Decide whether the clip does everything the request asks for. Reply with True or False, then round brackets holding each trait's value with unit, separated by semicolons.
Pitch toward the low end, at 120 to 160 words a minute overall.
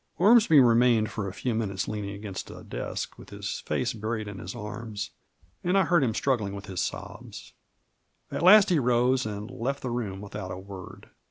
False (110 Hz; 190 wpm)